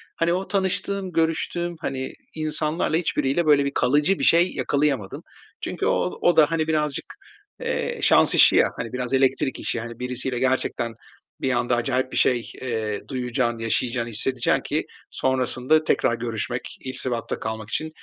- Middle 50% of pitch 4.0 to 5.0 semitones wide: Yes, average, 4.6 semitones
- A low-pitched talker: Yes, low, 130 Hz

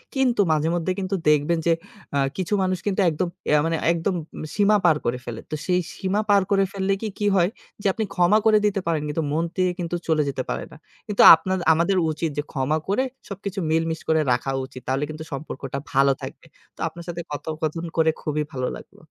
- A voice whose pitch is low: No, medium, 165 Hz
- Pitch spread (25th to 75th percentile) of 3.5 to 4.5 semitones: Yes, average, 4.1 semitones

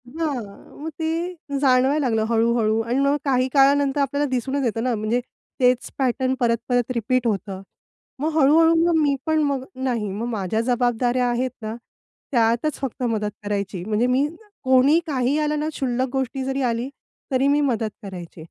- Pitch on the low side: No, very high, 255 Hz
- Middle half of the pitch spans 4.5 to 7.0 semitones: No, average, 3.3 semitones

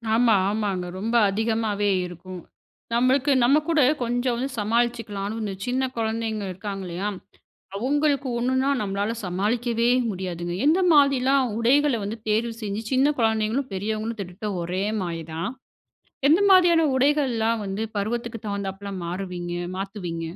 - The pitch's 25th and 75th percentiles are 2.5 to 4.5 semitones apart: Yes, average, 4.2 semitones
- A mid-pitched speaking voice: No, high, 220 Hz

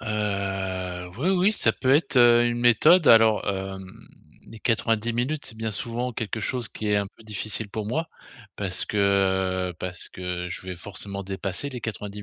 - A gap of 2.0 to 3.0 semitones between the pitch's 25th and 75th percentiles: No, average, 3.6 semitones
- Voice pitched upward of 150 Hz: No, low, 110 Hz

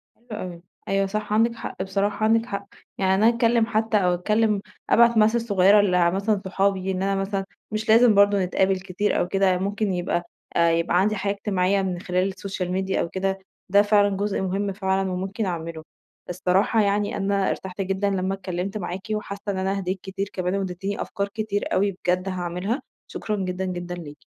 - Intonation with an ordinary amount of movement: No, narrow, 1.9 semitones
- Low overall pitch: No, high, 195 Hz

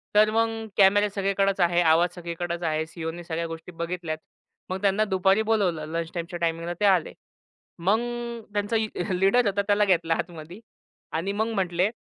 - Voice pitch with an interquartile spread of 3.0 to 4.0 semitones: Yes, average, 3.4 semitones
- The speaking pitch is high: No, medium, 180 Hz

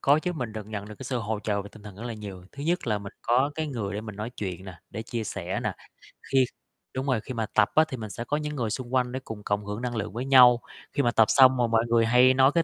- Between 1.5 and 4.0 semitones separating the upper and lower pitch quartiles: Yes, average, 3.5 semitones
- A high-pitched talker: No, low, 115 Hz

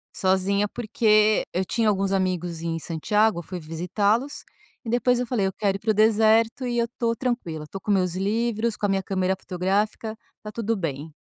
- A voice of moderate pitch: No, high, 205 Hz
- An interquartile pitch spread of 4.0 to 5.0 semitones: No, average, 3.4 semitones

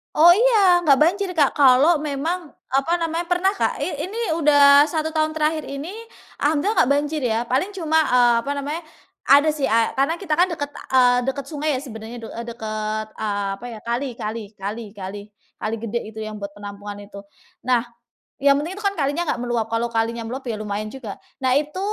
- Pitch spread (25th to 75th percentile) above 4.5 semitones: Yes, wide, 5.6 semitones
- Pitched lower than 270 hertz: No, very high, 275 Hz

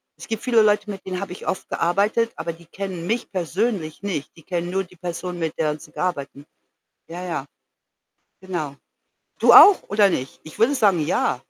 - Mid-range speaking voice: Yes, medium, 180 Hz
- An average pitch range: Yes, average, 3.8 semitones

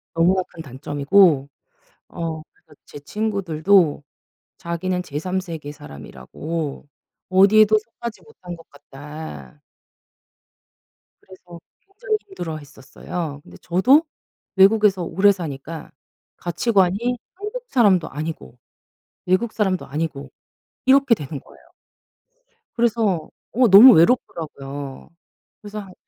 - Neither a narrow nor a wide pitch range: No, wide, 5.8 semitones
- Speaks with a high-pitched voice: No, medium, 180 Hz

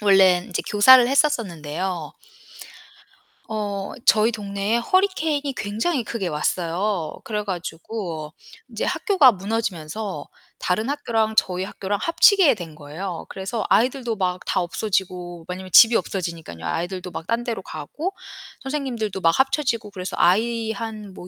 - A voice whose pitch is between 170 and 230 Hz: Yes, high, 205 Hz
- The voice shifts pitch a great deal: No, average, 4.5 semitones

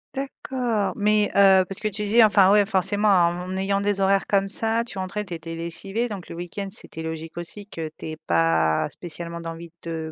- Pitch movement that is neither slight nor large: Yes, average, 3.6 semitones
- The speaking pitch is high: Yes, high, 195 Hz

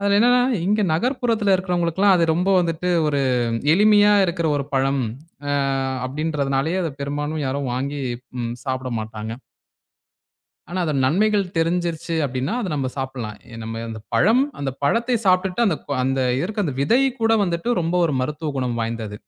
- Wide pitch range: Yes, wide, 6.3 semitones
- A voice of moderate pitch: Yes, medium, 160 Hz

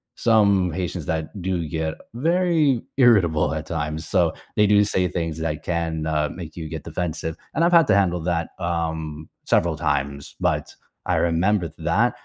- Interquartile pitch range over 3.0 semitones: Yes, average, 4.1 semitones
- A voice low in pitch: Yes, very low, 85 Hz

